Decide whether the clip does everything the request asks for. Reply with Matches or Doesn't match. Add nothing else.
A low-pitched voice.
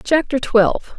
Doesn't match